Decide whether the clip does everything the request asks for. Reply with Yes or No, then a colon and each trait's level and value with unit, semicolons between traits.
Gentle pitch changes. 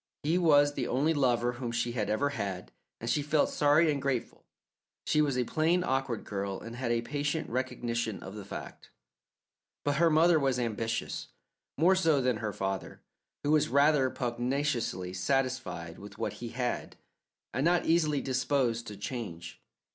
No: average, 4.1 semitones